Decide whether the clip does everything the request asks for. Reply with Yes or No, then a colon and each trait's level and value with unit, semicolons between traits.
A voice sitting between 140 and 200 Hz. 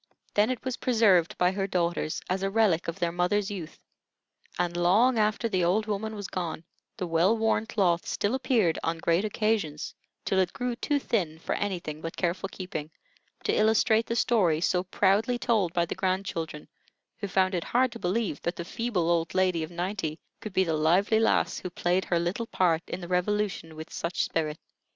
Yes: medium, 185 Hz